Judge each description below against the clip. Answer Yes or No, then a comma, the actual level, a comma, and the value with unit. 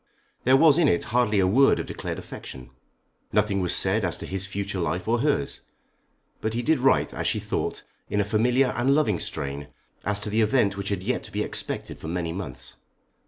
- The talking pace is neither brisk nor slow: No, fast, 210 wpm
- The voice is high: No, low, 105 Hz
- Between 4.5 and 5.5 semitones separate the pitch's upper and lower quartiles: Yes, average, 4.9 semitones